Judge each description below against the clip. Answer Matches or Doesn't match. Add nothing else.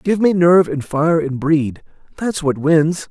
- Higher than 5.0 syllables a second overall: Doesn't match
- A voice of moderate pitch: Matches